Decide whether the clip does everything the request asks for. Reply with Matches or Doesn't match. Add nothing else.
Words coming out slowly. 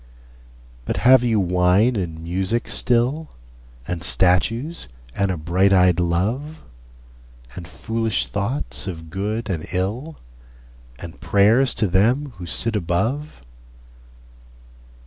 Matches